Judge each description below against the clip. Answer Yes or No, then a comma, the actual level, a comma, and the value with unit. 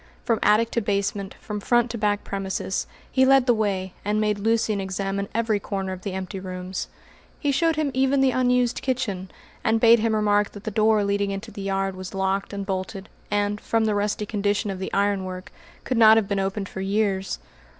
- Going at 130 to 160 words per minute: No, average, 200 wpm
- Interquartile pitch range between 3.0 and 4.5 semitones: No, narrow, 2.5 semitones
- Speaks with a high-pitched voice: Yes, high, 205 Hz